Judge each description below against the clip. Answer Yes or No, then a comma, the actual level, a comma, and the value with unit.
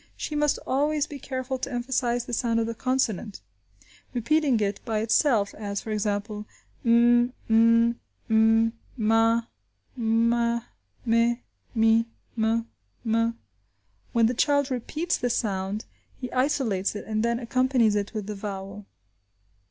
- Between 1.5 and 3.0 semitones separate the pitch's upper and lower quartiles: Yes, narrow, 2.4 semitones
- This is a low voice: No, high, 230 Hz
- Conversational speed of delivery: No, slow, 130 wpm